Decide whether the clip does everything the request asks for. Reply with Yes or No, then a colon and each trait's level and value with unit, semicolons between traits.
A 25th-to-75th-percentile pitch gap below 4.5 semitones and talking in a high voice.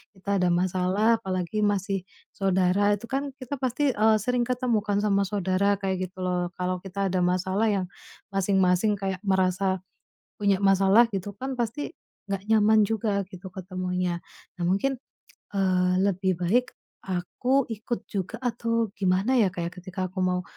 Yes: average, 2.9 semitones; high, 195 Hz